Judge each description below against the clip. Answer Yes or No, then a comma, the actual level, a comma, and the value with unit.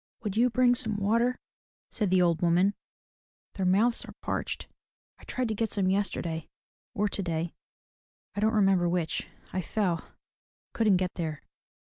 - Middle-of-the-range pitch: No, high, 195 Hz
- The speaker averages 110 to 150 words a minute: No, average, 165 wpm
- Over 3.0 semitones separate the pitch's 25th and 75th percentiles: Yes, average, 3.7 semitones